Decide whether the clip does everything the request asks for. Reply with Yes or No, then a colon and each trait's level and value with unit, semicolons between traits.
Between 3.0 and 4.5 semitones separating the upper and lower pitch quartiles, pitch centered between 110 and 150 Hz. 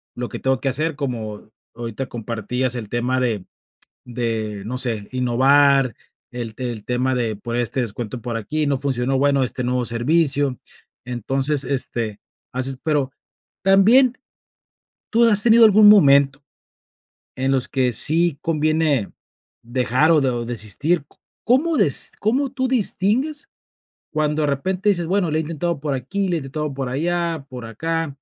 No: average, 5.0 semitones; low, 135 Hz